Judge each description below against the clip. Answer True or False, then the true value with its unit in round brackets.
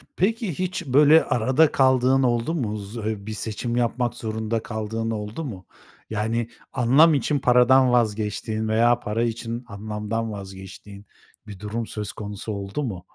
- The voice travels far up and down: False (3.3 semitones)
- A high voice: False (115 Hz)